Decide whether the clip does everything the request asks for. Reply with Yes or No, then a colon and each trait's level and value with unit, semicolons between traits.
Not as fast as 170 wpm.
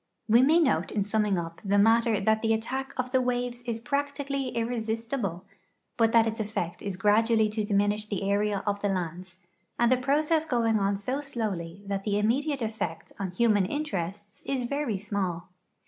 No: average, 175 wpm